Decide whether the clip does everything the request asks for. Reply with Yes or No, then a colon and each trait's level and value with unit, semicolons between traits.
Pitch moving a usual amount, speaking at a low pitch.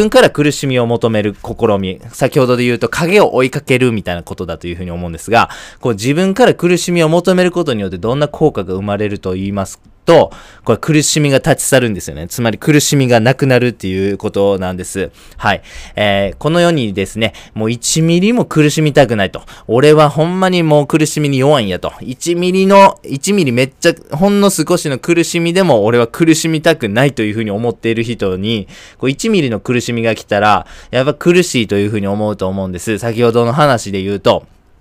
No: wide, 7.2 semitones; low, 120 Hz